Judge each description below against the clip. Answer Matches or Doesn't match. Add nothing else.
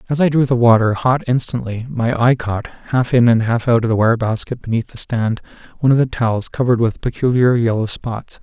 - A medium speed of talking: Doesn't match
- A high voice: Doesn't match